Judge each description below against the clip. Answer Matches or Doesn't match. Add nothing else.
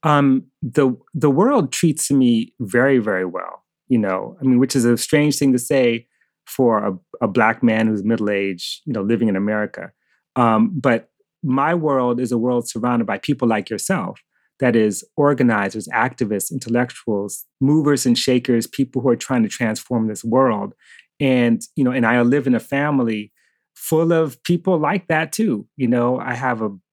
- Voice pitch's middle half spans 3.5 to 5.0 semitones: Matches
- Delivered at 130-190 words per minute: Matches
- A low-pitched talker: Matches